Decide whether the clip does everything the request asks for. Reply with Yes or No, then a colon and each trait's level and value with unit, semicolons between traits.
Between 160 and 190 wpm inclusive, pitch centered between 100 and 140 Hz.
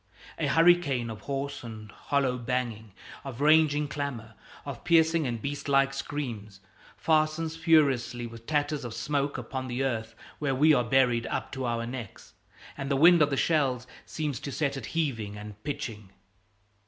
Yes: average, 165 wpm; low, 135 Hz